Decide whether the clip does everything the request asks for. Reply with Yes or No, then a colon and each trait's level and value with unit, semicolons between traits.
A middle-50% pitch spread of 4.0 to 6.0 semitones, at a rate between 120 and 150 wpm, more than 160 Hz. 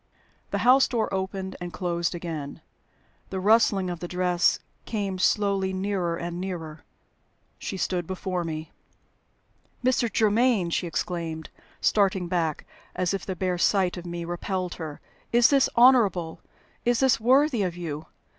No: average, 3.1 semitones; average, 145 wpm; medium, 185 Hz